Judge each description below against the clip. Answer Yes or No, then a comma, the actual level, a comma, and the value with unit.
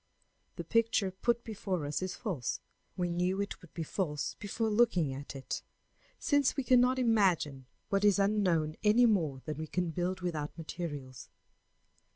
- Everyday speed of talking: Yes, average, 160 wpm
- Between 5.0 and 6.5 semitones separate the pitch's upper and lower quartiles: Yes, wide, 5.6 semitones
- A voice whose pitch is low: No, medium, 185 Hz